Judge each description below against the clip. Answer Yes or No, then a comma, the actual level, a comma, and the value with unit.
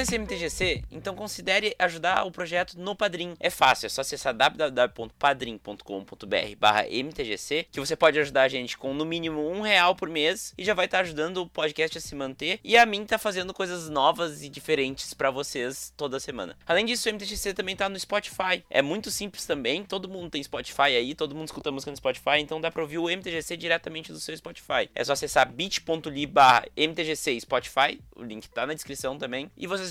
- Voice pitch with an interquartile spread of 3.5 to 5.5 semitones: Yes, average, 4.9 semitones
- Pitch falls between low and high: Yes, medium, 160 Hz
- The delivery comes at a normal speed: No, fast, 200 wpm